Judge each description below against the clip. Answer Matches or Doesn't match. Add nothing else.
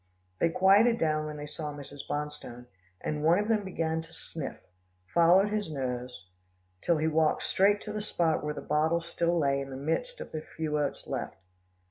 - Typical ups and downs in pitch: Matches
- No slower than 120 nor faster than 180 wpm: Doesn't match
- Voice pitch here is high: Doesn't match